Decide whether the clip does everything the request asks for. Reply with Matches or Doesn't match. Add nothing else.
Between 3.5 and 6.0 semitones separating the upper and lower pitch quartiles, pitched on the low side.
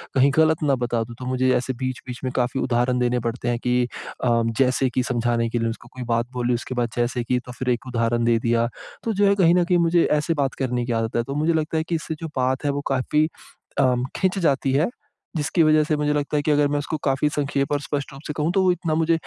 Matches